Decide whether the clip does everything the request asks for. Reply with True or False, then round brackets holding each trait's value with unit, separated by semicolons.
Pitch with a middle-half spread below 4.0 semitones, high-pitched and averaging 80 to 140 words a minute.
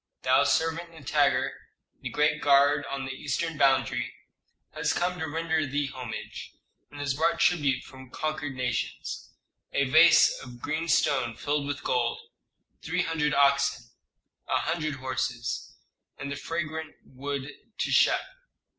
False (3.1 semitones; 145 Hz; 135 wpm)